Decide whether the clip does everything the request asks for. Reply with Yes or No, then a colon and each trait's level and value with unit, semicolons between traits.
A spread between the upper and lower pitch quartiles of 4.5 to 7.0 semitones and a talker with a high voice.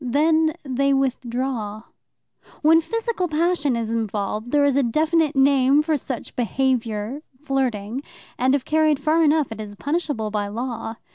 Yes: average, 4.8 semitones; very high, 270 Hz